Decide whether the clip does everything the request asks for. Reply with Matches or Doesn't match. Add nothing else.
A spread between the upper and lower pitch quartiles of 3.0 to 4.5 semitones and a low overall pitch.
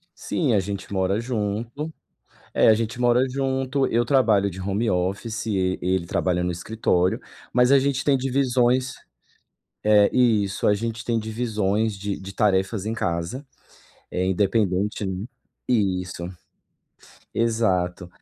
Matches